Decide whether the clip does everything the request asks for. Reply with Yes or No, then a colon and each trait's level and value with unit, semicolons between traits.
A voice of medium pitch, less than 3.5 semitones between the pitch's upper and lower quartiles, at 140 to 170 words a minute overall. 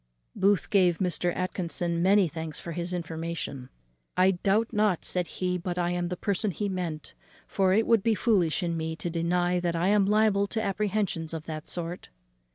No: medium, 180 Hz; average, 2.9 semitones; average, 180 wpm